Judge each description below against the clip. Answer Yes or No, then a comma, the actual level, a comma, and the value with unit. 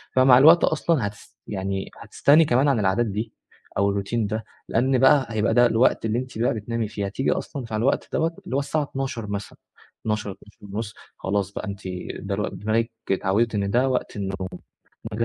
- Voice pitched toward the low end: Yes, low, 110 Hz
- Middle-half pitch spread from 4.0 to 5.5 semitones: Yes, average, 4.3 semitones